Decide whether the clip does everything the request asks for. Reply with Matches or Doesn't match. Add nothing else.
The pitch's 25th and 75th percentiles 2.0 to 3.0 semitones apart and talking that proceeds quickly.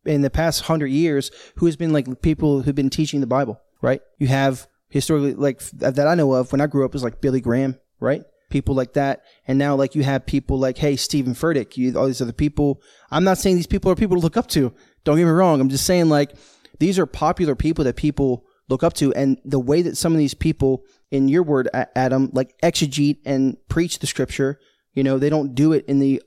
Matches